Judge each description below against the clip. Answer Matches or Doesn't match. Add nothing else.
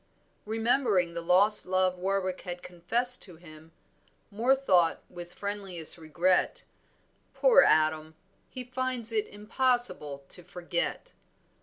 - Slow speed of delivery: Matches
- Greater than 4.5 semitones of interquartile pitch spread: Matches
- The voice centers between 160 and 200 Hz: Matches